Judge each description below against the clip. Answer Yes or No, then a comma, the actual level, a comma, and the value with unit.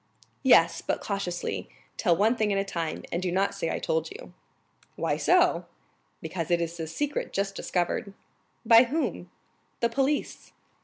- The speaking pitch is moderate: No, high, 195 Hz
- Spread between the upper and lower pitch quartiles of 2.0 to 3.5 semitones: No, average, 4.9 semitones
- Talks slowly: No, average, 160 wpm